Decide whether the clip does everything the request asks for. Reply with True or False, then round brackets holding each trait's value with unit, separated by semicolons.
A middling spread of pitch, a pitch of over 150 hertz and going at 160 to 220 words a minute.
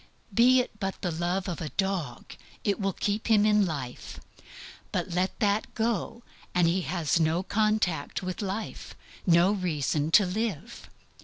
False (3.7 semitones; 190 Hz; 150 wpm)